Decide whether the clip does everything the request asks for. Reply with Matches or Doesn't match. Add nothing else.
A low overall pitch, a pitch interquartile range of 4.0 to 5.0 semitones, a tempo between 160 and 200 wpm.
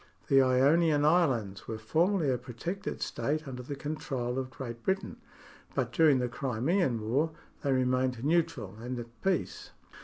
Doesn't match